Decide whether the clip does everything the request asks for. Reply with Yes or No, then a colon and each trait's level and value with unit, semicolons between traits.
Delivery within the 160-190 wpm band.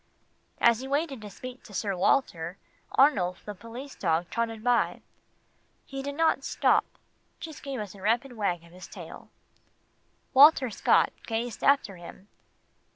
No: average, 150 wpm